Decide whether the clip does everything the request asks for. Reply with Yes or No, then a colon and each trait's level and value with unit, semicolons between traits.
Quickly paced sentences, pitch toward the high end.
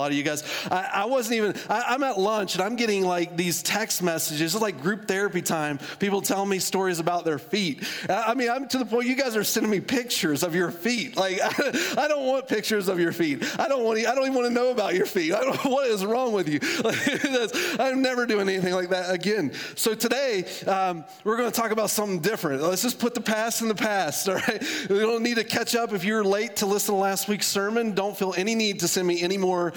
Yes: fast, 260 wpm; high, 205 Hz